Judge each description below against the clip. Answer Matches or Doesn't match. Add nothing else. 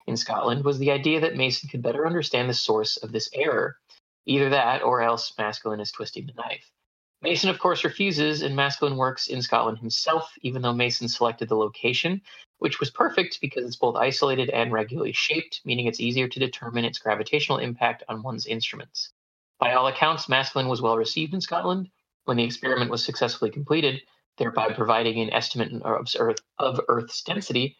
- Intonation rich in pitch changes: Doesn't match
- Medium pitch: Doesn't match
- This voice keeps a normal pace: Matches